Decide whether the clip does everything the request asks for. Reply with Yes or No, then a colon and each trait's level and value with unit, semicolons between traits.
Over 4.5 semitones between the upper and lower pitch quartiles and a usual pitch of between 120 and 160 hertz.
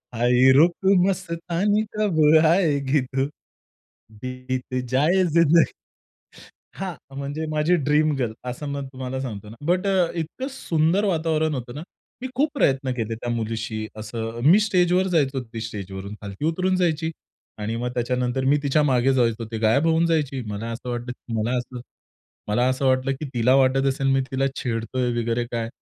Yes: average, 5.1 semitones; low, 135 Hz